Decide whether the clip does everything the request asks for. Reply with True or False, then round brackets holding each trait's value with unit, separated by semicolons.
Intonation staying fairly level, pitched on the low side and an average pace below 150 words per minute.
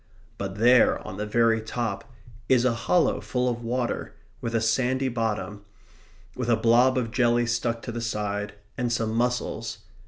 False (1.7 semitones; 115 Hz; 165 wpm)